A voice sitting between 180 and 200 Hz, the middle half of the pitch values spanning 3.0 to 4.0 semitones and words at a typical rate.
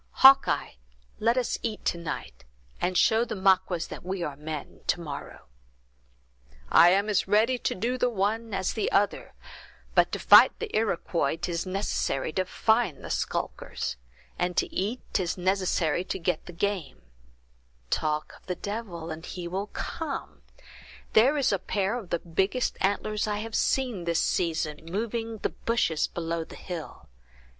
No: high, 190 Hz; average, 4.7 semitones; average, 160 wpm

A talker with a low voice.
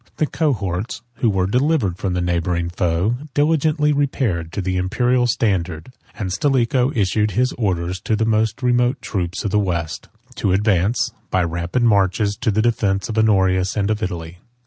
Yes: low, 100 Hz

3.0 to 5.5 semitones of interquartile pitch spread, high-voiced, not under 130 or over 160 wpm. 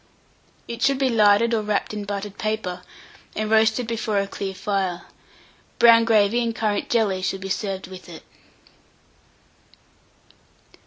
No: narrow, 2.6 semitones; high, 210 Hz; average, 140 wpm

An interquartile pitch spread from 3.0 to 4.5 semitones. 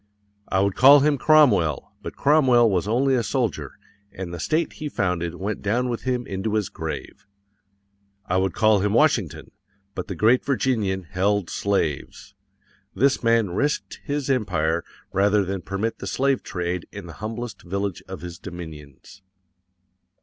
No: wide, 5.5 semitones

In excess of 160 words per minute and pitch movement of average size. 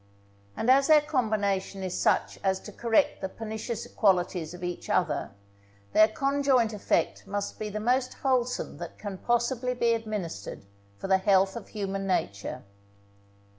No: average, 150 wpm; average, 4.0 semitones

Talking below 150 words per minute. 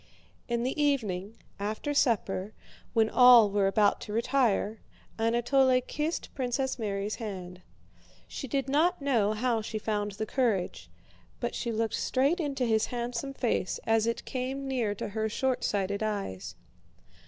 Yes: average, 140 wpm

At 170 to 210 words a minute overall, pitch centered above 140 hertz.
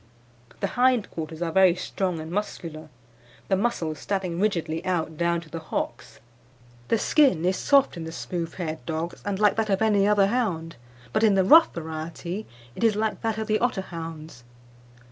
Yes: average, 180 wpm; medium, 185 Hz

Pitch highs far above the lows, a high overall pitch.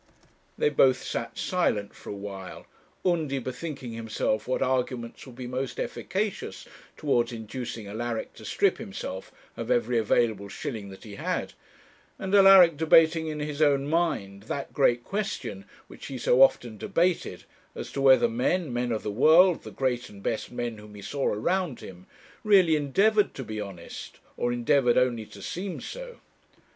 No: wide, 6.3 semitones; low, 130 Hz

